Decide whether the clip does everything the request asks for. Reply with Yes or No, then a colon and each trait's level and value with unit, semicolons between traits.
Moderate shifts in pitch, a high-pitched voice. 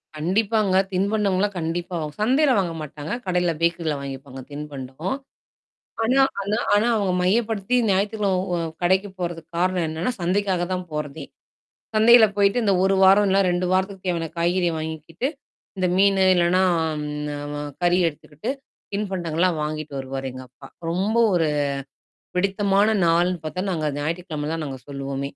No: average, 4.3 semitones; medium, 180 Hz